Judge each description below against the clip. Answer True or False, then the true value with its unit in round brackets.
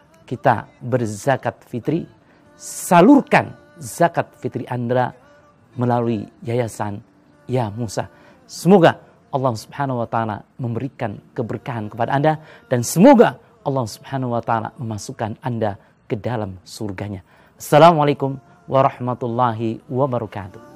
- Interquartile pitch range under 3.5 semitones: False (3.8 semitones)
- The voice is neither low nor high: False (125 Hz)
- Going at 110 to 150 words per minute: False (100 wpm)